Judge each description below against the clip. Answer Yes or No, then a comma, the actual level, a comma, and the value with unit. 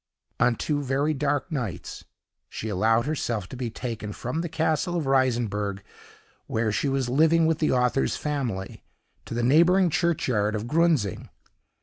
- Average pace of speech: Yes, average, 150 wpm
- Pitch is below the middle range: Yes, low, 130 Hz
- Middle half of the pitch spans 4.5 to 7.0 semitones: Yes, wide, 5.5 semitones